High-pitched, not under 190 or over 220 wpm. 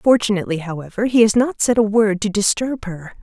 Yes: high, 210 Hz; fast, 205 wpm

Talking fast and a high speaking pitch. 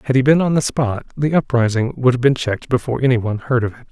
No: fast, 275 wpm; low, 125 Hz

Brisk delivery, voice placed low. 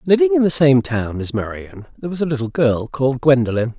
Yes: fast, 220 wpm; low, 125 Hz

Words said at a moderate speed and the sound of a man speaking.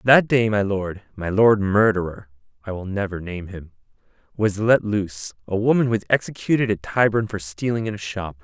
Yes: average, 165 wpm; male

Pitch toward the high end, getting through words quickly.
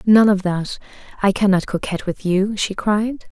No: high, 200 Hz; average, 160 wpm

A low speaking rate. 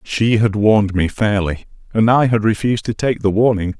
No: fast, 205 wpm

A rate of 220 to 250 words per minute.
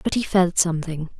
No: average, 200 wpm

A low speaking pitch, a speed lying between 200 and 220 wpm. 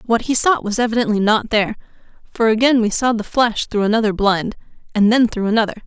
No: high, 220 Hz; fast, 205 wpm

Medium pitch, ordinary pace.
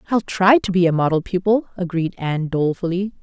Yes: medium, 180 Hz; average, 185 wpm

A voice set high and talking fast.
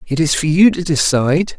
No: medium, 160 Hz; fast, 225 wpm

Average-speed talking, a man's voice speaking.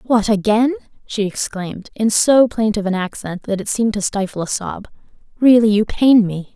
No: average, 185 wpm; female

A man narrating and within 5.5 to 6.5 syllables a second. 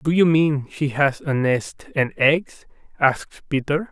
No: male; 3.8 syllables/s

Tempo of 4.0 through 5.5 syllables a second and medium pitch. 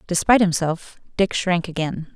Yes: 5.0 syllables/s; medium, 175 Hz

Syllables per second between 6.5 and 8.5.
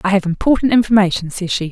Yes: 6.6 syllables/s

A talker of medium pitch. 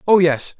Yes: medium, 170 Hz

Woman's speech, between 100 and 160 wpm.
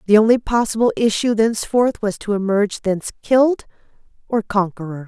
Yes: female; average, 140 wpm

